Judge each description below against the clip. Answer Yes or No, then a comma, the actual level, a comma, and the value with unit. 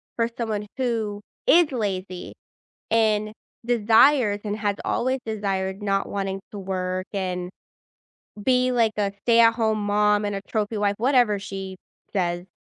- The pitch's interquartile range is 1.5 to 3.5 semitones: Yes, average, 2.7 semitones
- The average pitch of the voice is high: Yes, high, 210 Hz